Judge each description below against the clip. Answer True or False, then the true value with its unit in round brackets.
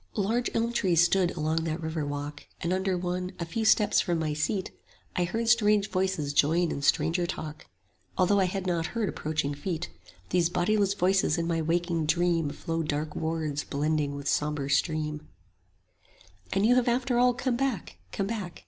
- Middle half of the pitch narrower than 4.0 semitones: False (4.3 semitones)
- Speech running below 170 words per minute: False (180 wpm)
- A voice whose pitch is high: False (175 Hz)